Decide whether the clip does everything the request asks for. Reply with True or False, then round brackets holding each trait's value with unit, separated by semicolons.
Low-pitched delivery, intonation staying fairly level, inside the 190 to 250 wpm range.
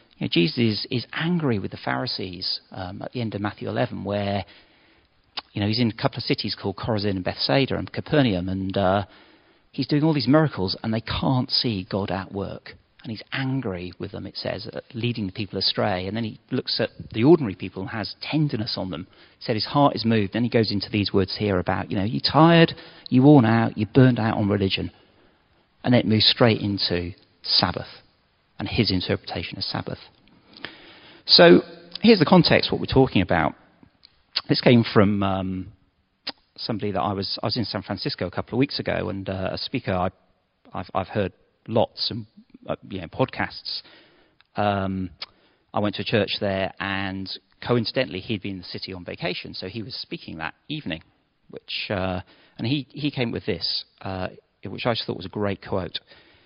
False (105 Hz; 4.3 semitones; 200 wpm)